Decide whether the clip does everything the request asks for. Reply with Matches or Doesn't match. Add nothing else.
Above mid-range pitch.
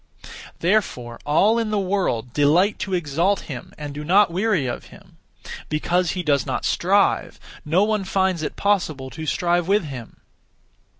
Doesn't match